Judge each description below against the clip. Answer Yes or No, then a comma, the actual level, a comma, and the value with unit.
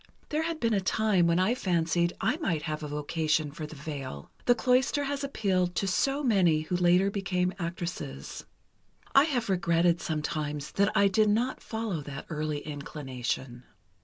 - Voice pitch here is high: No, medium, 175 Hz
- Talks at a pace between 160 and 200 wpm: Yes, average, 165 wpm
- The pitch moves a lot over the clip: Yes, wide, 5.9 semitones